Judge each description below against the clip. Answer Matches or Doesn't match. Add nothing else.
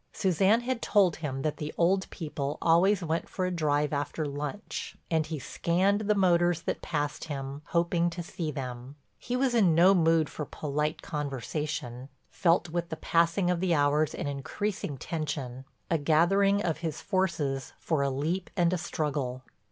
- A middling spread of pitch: Matches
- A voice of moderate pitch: Matches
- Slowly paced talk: Doesn't match